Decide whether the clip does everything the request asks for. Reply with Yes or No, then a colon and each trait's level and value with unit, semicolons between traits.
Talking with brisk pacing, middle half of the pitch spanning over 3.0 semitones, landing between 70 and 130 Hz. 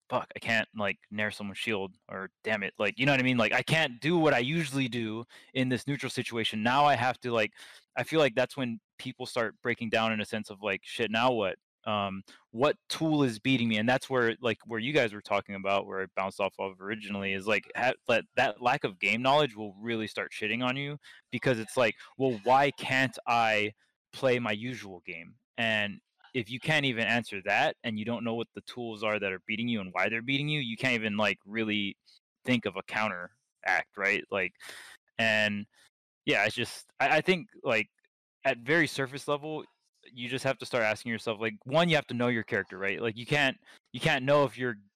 Yes: fast, 225 wpm; average, 3.7 semitones; low, 120 Hz